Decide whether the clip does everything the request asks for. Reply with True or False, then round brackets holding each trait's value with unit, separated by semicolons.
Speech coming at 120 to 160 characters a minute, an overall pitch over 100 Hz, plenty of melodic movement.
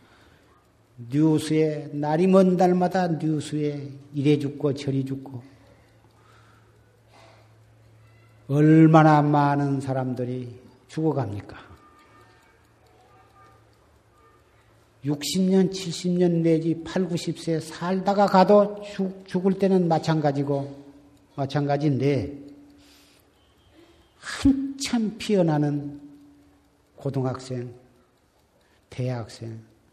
True (145 characters per minute; 140 Hz; 5.9 semitones)